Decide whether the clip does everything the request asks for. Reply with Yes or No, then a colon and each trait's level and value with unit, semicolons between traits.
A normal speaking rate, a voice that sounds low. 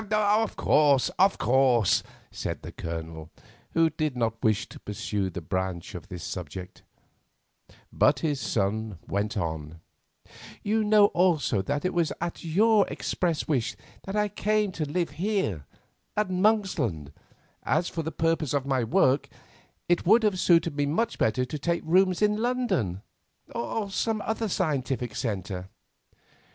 No: average, 145 wpm; medium, 150 Hz